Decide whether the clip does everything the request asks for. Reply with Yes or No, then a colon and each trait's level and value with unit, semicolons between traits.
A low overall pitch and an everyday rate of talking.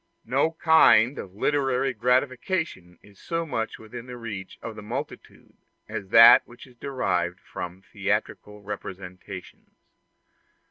No: low, 115 Hz; slow, 125 wpm